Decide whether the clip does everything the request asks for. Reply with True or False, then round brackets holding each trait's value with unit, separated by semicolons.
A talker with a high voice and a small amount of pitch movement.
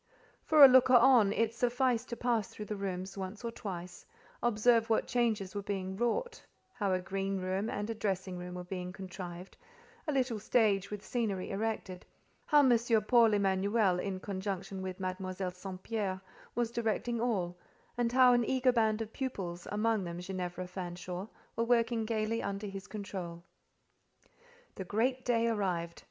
False (205 Hz; 3.8 semitones)